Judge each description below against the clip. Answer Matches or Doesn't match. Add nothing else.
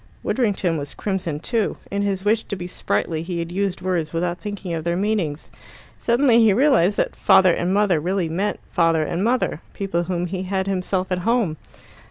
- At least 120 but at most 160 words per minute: Doesn't match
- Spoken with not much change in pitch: Doesn't match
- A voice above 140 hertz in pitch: Matches